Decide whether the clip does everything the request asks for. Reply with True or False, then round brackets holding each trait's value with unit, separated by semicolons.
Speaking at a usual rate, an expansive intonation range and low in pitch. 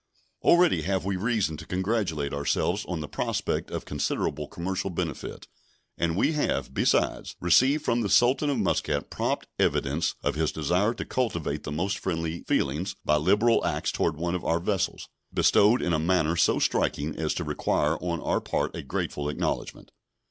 False (170 wpm; 4.5 semitones; 90 Hz)